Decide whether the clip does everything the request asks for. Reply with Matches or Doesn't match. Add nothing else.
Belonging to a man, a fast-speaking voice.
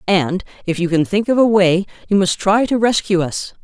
Doesn't match